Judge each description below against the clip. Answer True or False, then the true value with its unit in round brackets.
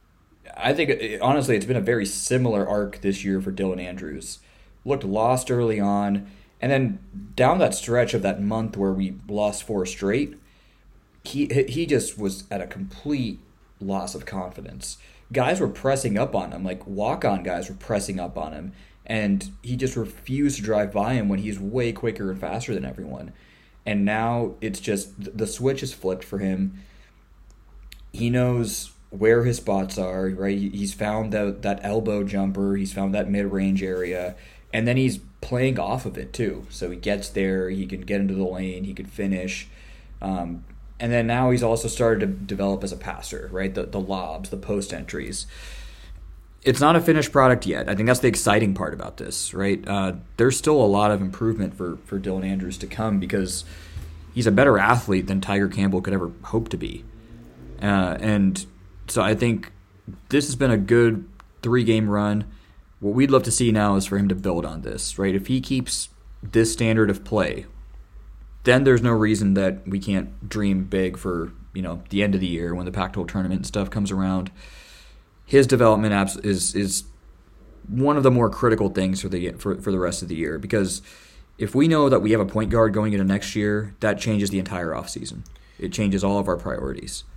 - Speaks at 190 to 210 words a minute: True (195 wpm)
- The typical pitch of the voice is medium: False (100 Hz)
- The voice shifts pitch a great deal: False (3.0 semitones)